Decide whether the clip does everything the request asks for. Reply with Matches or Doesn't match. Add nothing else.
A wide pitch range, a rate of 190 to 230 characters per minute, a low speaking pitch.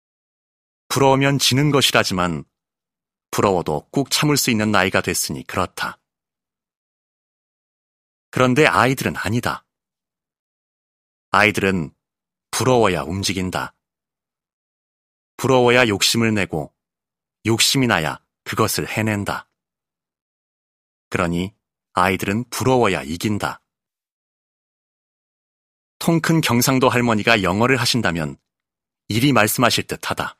Matches